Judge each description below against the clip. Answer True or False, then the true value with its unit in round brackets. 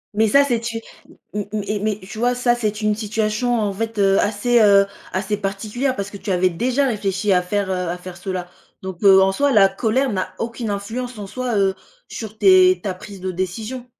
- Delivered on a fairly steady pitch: False (3.3 semitones)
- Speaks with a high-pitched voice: True (210 Hz)